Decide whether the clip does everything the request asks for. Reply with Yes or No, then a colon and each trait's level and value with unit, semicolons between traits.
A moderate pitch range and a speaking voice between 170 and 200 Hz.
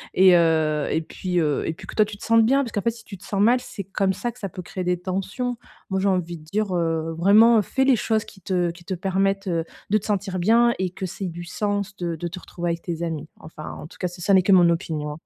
Yes: average, 3.2 semitones; medium, 185 Hz